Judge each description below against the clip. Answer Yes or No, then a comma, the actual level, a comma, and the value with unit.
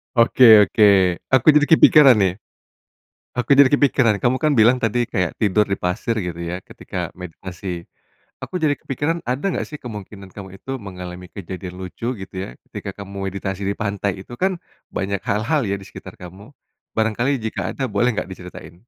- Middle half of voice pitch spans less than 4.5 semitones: No, average, 5.0 semitones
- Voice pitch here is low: Yes, low, 105 Hz